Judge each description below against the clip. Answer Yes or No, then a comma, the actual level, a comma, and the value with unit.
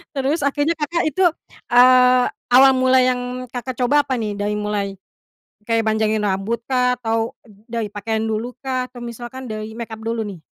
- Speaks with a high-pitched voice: Yes, high, 235 Hz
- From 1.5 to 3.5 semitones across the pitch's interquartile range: Yes, average, 2.8 semitones